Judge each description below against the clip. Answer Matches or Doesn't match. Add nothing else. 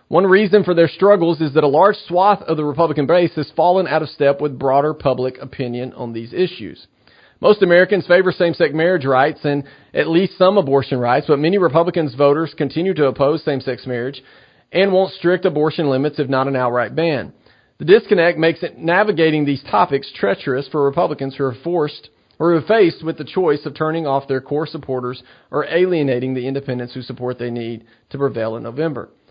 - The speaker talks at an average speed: Matches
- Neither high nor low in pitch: Matches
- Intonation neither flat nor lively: Matches